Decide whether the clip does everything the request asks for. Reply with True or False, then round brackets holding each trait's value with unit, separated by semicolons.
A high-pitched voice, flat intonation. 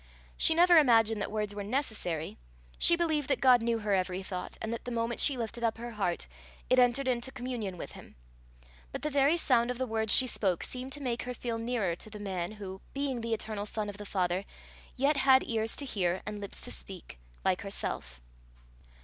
False (230 Hz; 3.9 semitones)